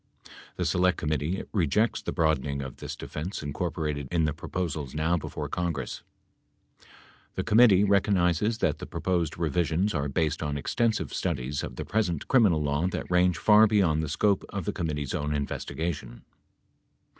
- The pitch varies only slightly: No, average, 4.0 semitones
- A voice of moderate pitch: No, very low, 80 Hz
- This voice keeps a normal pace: Yes, average, 170 wpm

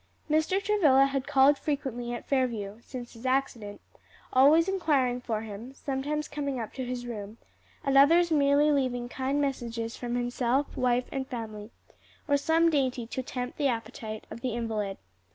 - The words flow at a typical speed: Yes, average, 160 wpm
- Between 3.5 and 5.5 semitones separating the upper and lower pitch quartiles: No, average, 3.1 semitones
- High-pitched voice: Yes, very high, 260 Hz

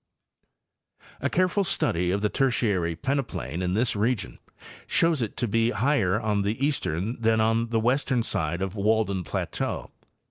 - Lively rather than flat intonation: No, average, 4.7 semitones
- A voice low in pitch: Yes, low, 110 Hz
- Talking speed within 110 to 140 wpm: No, average, 150 wpm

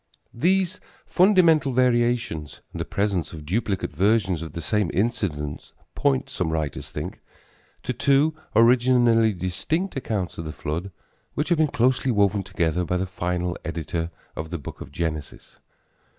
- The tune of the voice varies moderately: No, wide, 7.3 semitones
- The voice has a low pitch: Yes, low, 100 Hz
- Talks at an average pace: Yes, average, 150 wpm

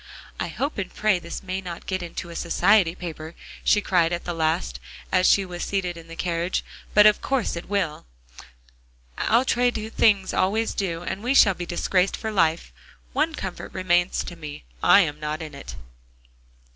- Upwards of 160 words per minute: Yes, average, 180 wpm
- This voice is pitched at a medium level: Yes, medium, 180 Hz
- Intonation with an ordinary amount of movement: Yes, average, 3.3 semitones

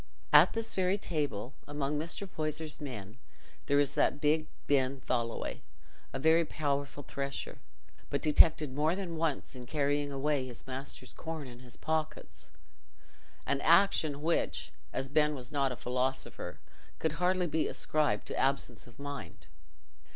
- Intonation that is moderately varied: Yes, average, 3.2 semitones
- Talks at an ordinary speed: Yes, average, 145 wpm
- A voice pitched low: No, medium, 145 Hz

